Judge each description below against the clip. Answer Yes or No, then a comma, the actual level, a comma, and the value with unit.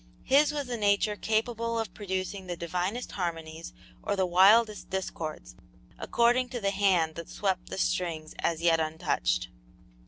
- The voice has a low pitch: No, high, 190 Hz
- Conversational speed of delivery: Yes, average, 150 wpm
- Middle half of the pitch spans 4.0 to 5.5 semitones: Yes, average, 4.9 semitones